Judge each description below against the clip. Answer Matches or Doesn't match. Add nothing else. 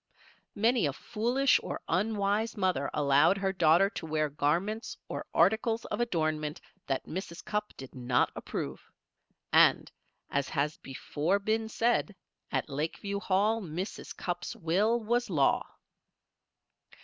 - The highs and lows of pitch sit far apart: Matches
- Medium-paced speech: Doesn't match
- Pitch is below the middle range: Doesn't match